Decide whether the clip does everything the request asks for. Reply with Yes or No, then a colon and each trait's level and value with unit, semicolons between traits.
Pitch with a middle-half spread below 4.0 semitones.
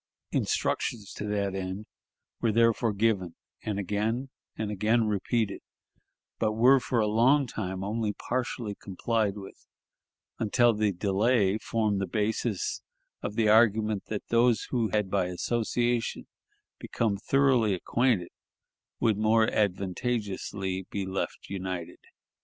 Yes: average, 2.8 semitones